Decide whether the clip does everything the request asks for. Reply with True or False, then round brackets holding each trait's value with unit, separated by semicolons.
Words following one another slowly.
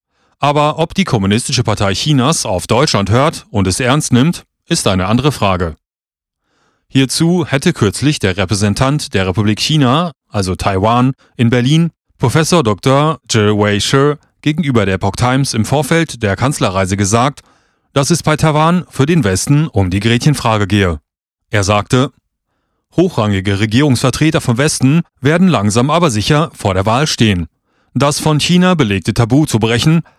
False (145 wpm)